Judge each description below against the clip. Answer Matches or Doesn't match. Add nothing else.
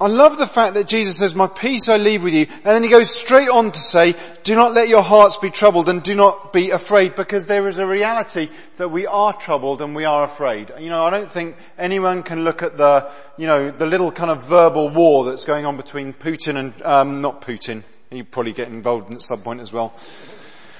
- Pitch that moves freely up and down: Matches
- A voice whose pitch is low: Doesn't match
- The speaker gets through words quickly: Matches